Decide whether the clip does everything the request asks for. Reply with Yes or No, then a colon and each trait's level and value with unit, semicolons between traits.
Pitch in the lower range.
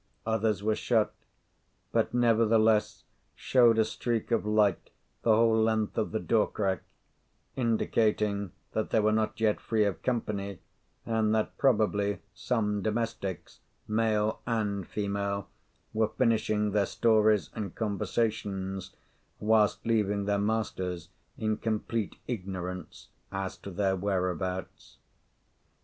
Yes: low, 105 Hz